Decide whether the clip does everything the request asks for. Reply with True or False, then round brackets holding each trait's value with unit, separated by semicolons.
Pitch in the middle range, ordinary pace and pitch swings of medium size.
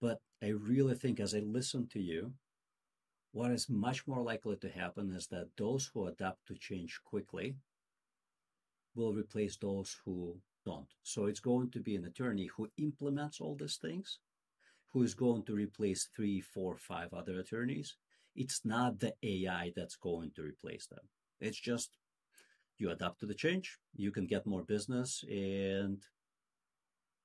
False (105 Hz; 160 wpm; 4.1 semitones)